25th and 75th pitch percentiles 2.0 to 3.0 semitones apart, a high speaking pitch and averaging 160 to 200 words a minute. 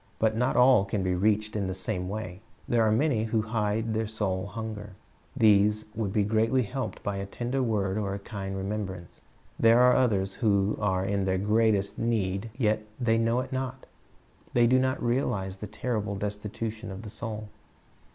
No: narrow, 2.6 semitones; low, 110 Hz; average, 180 wpm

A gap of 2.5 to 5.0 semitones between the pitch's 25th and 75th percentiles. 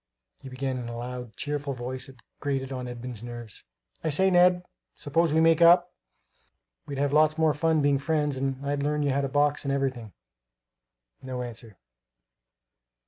Yes: average, 3.0 semitones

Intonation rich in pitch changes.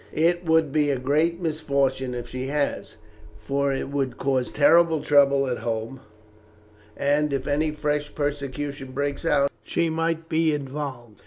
No: narrow, 2.4 semitones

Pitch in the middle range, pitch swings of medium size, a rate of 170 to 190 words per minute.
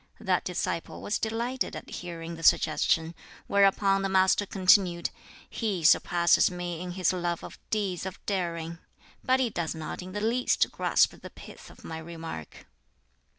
No: medium, 180 Hz; average, 3.0 semitones; average, 155 wpm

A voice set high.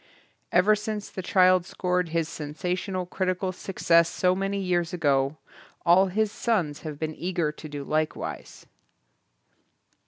No: medium, 180 Hz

